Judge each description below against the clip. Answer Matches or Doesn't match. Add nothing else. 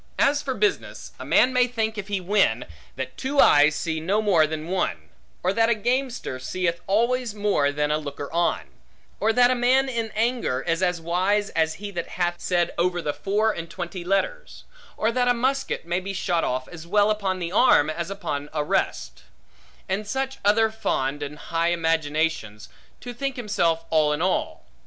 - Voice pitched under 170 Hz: Doesn't match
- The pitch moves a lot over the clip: Matches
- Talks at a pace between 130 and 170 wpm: Doesn't match